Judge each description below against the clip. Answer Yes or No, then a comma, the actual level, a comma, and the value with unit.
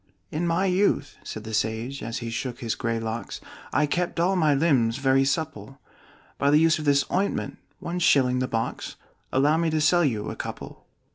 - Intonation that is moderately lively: No, wide, 5.8 semitones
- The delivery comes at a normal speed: Yes, average, 195 wpm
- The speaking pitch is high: No, medium, 140 Hz